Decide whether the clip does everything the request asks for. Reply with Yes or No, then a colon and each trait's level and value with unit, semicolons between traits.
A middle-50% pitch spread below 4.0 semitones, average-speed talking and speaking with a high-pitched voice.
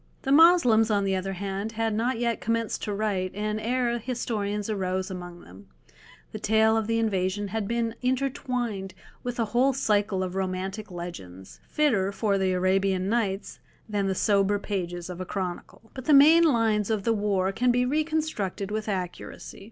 Yes: average, 3.5 semitones; average, 175 wpm; high, 210 Hz